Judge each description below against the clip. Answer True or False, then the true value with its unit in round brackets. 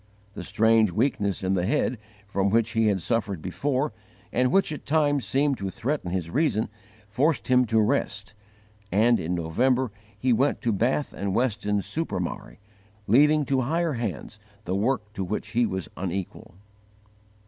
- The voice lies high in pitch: False (110 Hz)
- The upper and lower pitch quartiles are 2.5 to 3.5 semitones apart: False (5.3 semitones)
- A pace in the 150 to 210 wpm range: True (160 wpm)